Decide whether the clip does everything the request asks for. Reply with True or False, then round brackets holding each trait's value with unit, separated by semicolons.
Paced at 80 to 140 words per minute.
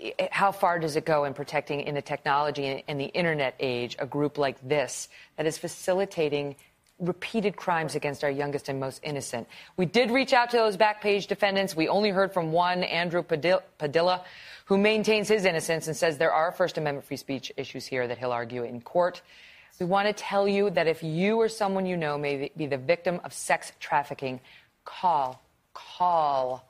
False (190 wpm)